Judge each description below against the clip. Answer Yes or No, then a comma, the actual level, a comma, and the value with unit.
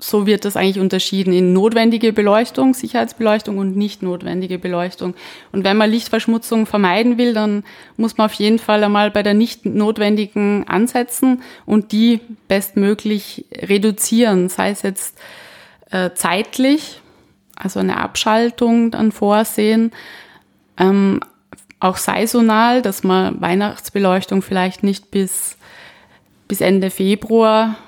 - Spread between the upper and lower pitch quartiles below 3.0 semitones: Yes, narrow, 2.6 semitones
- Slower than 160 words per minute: Yes, slow, 125 wpm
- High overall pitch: Yes, high, 210 Hz